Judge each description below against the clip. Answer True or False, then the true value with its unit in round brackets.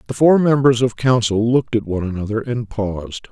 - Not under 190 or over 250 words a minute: True (200 wpm)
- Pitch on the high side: False (115 Hz)